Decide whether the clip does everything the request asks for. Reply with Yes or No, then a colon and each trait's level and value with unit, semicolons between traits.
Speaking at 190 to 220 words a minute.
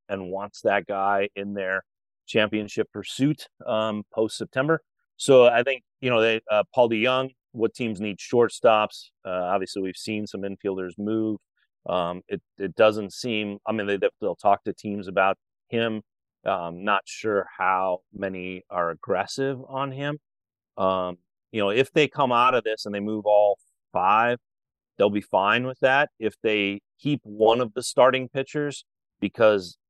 No: average, 165 wpm